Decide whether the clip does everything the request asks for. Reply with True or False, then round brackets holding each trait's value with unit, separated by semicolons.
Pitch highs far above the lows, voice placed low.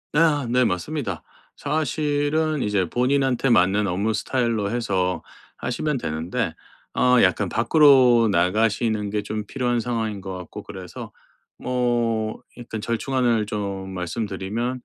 False (4.2 semitones; 115 Hz)